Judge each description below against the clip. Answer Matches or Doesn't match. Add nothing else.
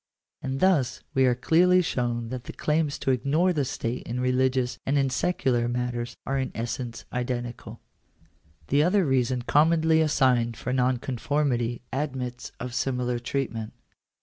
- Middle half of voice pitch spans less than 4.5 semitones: Matches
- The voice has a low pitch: Matches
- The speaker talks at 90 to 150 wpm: Matches